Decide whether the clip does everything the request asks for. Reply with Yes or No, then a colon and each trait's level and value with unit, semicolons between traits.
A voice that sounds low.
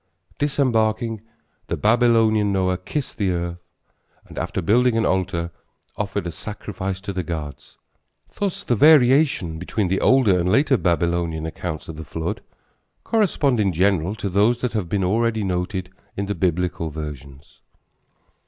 Yes: very low, 95 Hz